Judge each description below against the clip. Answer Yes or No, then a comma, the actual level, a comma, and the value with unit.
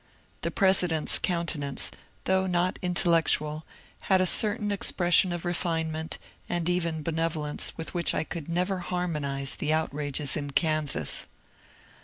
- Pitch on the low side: No, medium, 165 Hz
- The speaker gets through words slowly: Yes, slow, 125 wpm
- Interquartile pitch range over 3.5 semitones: No, average, 2.7 semitones